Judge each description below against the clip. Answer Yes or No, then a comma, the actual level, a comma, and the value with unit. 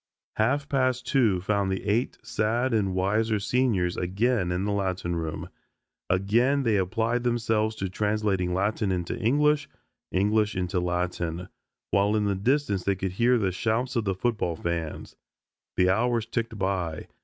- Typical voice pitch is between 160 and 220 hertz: No, low, 105 Hz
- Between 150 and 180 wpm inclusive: Yes, average, 155 wpm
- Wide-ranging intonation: No, average, 4.0 semitones